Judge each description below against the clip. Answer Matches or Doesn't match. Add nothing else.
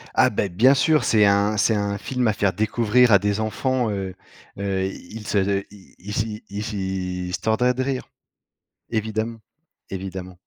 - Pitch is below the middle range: Matches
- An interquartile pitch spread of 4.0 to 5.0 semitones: Doesn't match